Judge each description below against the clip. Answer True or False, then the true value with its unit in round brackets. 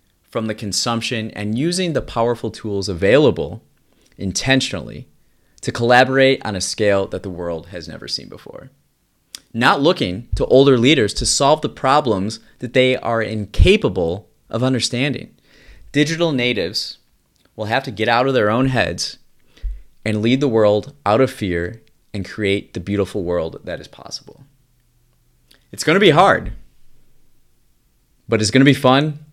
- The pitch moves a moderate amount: True (4.6 semitones)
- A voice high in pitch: False (115 Hz)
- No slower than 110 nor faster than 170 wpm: True (145 wpm)